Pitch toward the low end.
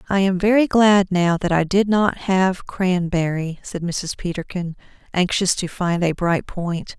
No: medium, 185 Hz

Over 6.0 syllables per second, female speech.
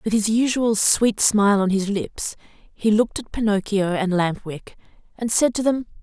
No: 4.6 syllables/s; female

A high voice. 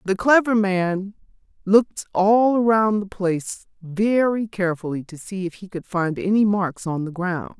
Yes: high, 195 Hz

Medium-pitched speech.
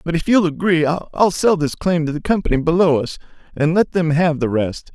Yes: medium, 165 Hz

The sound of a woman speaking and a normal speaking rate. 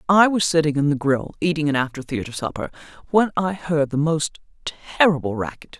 Yes: female; average, 185 wpm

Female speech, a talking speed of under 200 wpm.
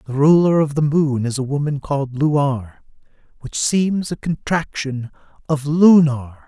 No: male; average, 150 wpm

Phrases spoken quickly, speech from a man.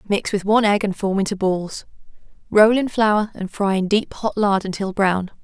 No: fast, 210 wpm; female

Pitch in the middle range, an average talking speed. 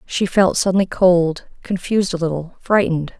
Yes: medium, 180 Hz; average, 150 wpm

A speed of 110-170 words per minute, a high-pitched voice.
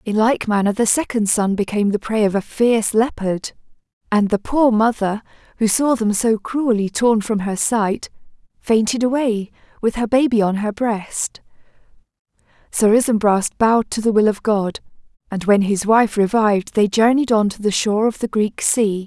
No: average, 180 wpm; high, 215 Hz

